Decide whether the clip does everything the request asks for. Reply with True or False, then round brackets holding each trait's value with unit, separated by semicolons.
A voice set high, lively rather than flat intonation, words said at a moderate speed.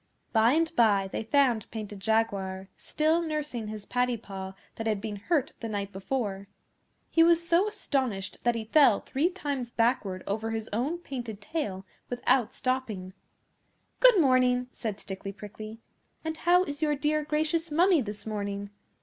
True (240 Hz; 6.6 semitones; 160 wpm)